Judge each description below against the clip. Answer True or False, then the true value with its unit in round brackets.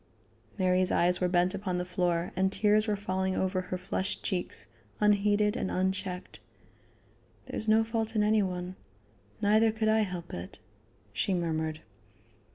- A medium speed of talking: True (155 wpm)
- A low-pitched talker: False (190 Hz)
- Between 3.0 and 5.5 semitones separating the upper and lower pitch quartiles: False (2.6 semitones)